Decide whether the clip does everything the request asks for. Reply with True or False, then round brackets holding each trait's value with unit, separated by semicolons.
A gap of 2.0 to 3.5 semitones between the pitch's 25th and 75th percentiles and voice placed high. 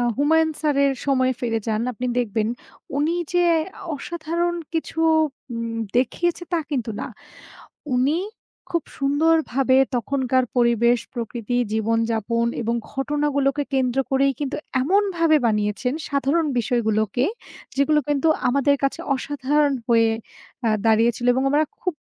False (4.2 semitones; 270 Hz)